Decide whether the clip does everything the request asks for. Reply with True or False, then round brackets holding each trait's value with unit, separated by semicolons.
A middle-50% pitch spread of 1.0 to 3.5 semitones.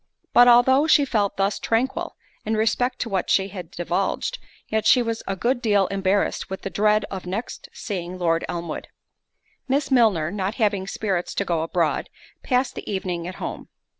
False (4.2 semitones)